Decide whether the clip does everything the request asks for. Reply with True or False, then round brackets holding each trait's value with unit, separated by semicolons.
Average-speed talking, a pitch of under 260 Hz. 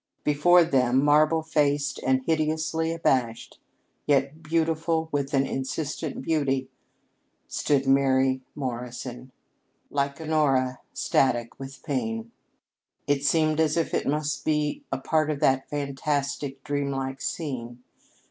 False (120 wpm; 140 Hz)